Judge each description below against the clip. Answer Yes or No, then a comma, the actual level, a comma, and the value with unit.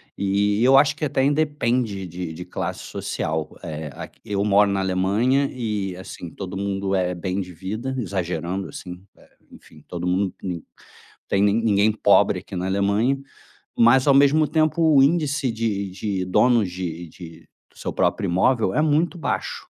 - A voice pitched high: No, low, 100 Hz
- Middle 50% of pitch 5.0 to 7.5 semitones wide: Yes, wide, 5.6 semitones